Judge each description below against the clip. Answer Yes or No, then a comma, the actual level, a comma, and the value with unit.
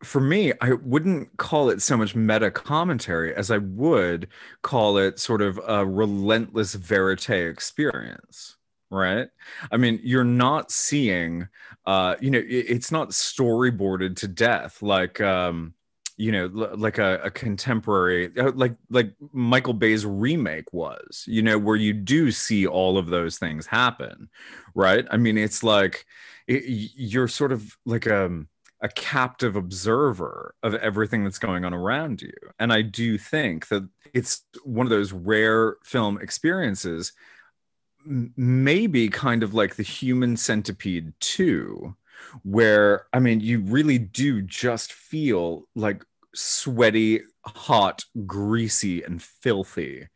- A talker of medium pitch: No, low, 110 Hz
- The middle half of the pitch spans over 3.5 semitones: Yes, average, 4.1 semitones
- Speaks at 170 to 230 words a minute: No, average, 140 wpm